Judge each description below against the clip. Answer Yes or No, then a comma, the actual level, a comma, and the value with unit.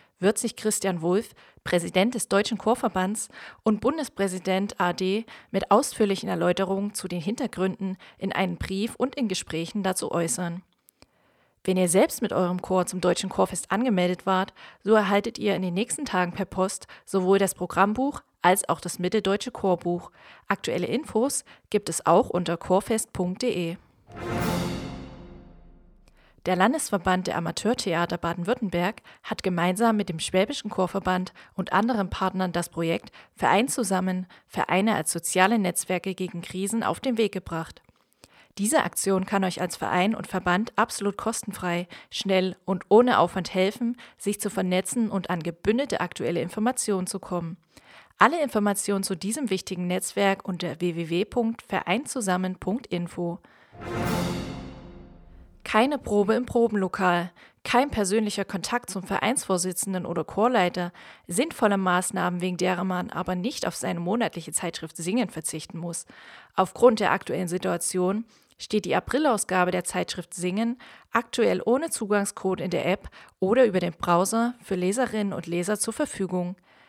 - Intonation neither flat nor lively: Yes, average, 3.2 semitones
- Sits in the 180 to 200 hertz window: Yes, high, 190 Hz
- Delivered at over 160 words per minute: No, average, 135 wpm